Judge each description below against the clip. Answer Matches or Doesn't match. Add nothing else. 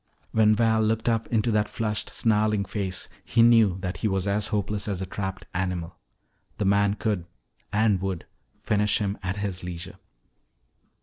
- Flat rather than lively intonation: Matches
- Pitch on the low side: Matches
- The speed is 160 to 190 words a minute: Matches